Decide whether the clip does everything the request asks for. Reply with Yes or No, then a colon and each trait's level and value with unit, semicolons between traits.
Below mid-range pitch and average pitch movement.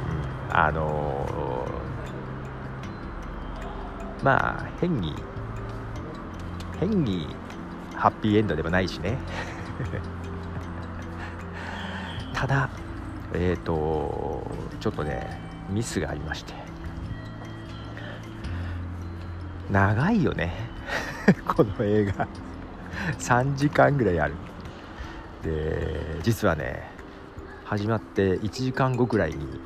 Yes: very low, 90 Hz; average, 4.4 semitones